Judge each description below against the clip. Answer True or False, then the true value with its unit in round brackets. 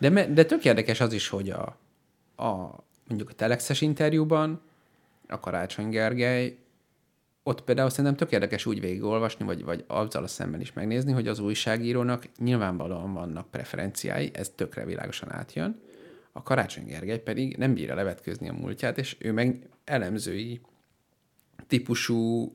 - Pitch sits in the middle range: False (120 Hz)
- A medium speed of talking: True (145 wpm)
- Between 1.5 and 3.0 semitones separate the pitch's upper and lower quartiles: False (3.6 semitones)